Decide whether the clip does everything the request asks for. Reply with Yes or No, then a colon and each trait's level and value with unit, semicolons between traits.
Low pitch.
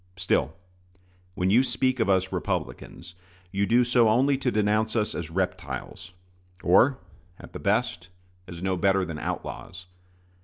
Yes: very low, 95 Hz